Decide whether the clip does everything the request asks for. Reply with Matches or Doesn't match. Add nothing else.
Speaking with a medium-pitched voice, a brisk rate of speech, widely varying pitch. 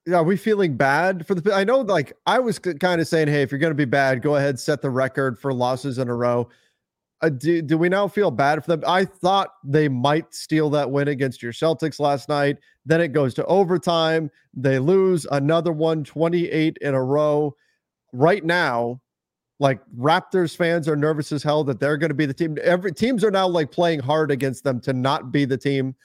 Doesn't match